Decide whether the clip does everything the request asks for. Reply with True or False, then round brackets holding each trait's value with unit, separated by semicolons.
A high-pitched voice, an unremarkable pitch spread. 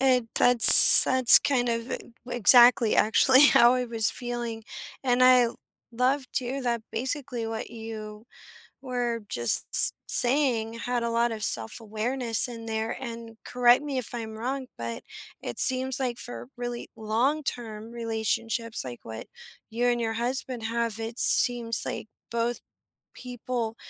False (235 Hz; 1.9 semitones)